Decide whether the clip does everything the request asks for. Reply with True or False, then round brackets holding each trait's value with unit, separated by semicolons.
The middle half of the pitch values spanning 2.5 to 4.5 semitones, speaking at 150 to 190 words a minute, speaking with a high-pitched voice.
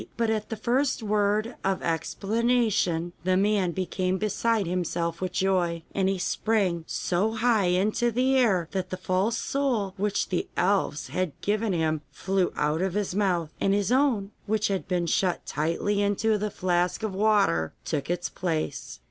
True (3.3 semitones; 165 wpm; 195 Hz)